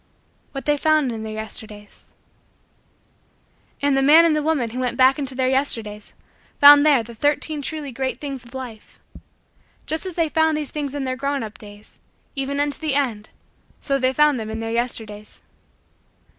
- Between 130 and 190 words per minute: Yes, average, 180 wpm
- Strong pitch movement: No, average, 4.2 semitones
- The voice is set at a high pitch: Yes, very high, 270 Hz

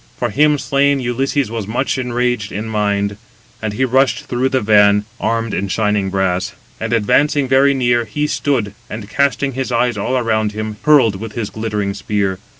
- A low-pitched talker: Yes, low, 115 Hz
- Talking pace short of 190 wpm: Yes, average, 175 wpm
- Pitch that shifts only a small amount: No, average, 4.1 semitones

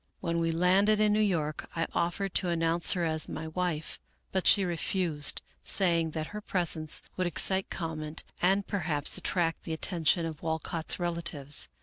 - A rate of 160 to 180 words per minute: Yes, average, 165 wpm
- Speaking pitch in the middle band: Yes, medium, 170 Hz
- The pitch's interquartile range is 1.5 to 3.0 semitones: Yes, narrow, 2.4 semitones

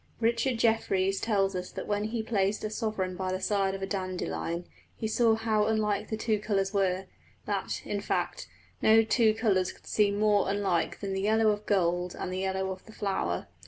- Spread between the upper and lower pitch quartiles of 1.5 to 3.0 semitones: Yes, narrow, 2.4 semitones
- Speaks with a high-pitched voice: Yes, high, 200 Hz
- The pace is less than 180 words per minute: No, average, 195 wpm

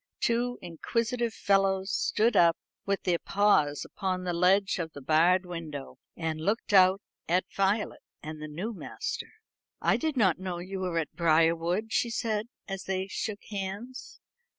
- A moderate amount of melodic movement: Yes, average, 3.8 semitones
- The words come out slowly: No, average, 155 wpm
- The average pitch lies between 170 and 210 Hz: Yes, high, 190 Hz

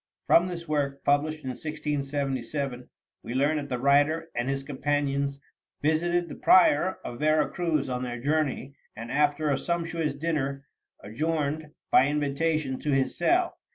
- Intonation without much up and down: Yes, narrow, 2.3 semitones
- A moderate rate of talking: Yes, average, 150 wpm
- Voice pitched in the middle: Yes, medium, 145 Hz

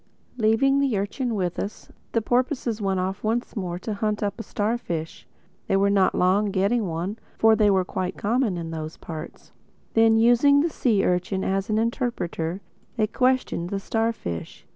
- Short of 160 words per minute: No, average, 170 wpm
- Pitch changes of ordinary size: Yes, average, 3.8 semitones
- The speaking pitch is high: Yes, high, 210 Hz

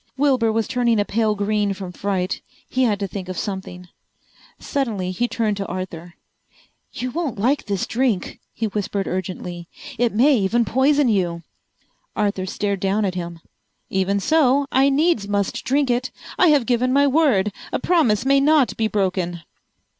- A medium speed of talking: Yes, average, 165 wpm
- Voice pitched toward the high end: Yes, high, 210 Hz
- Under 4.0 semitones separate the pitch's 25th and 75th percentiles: No, average, 5.2 semitones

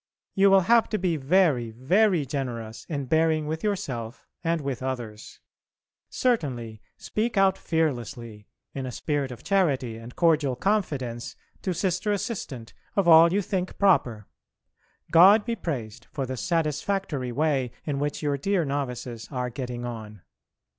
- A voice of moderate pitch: Yes, medium, 145 Hz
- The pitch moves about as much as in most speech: No, wide, 6.7 semitones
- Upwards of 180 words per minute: No, average, 145 wpm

